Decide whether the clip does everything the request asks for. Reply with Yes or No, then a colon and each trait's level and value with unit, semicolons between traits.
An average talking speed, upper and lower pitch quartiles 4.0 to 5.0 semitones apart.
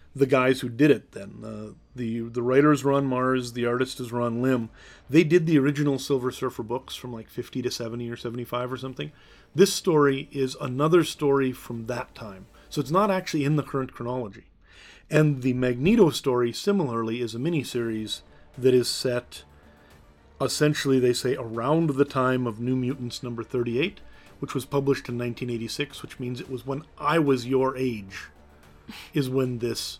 No: average, 185 wpm; average, 3.0 semitones